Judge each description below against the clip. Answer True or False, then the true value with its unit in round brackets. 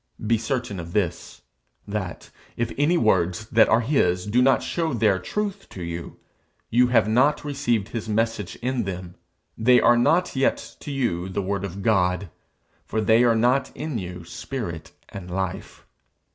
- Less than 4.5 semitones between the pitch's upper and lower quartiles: False (5.1 semitones)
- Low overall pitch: True (110 Hz)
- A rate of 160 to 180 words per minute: True (165 wpm)